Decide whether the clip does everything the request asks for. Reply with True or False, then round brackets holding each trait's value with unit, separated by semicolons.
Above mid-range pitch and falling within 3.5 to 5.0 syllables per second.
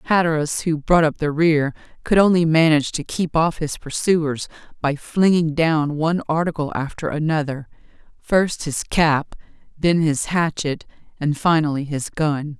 False (155 Hz; 4.5 syllables/s)